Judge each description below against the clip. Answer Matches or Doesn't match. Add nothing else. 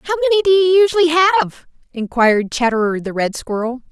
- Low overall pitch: Doesn't match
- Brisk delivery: Doesn't match